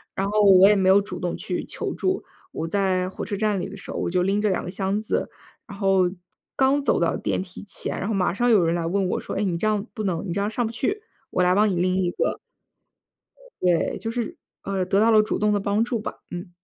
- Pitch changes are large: No, average, 2.7 semitones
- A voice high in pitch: Yes, high, 195 Hz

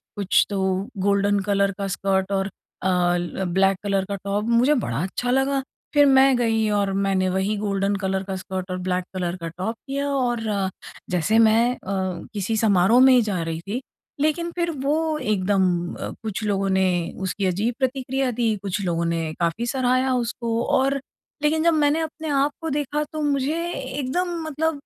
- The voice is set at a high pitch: Yes, high, 215 Hz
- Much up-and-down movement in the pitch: Yes, wide, 5.8 semitones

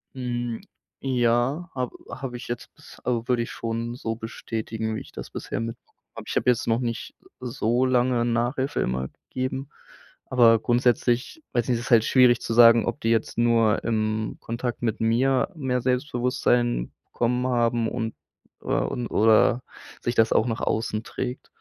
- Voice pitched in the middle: No, low, 120 Hz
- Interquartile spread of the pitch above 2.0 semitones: No, narrow, 1.7 semitones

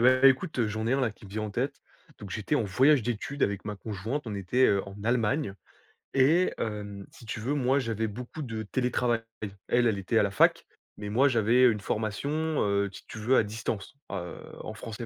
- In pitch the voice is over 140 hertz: No, low, 110 Hz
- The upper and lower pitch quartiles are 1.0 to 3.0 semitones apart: No, average, 3.7 semitones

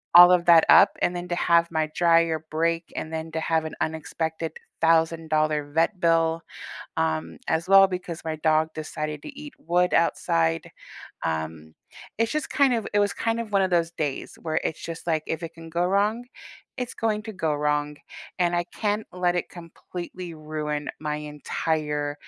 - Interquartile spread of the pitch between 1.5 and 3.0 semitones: Yes, narrow, 2.5 semitones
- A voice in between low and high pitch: Yes, medium, 165 Hz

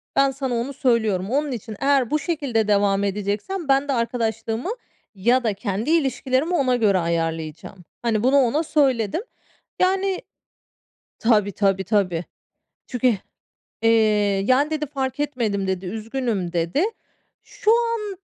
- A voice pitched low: No, high, 235 Hz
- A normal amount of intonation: No, wide, 5.7 semitones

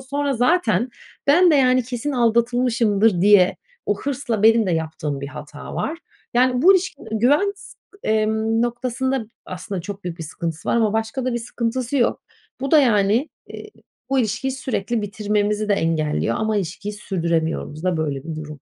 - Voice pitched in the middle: No, high, 220 Hz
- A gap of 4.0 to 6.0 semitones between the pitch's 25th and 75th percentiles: Yes, wide, 5.6 semitones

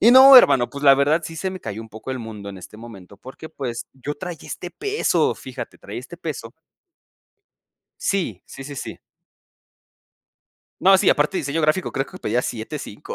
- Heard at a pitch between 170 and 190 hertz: No, medium, 140 Hz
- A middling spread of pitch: No, wide, 7.3 semitones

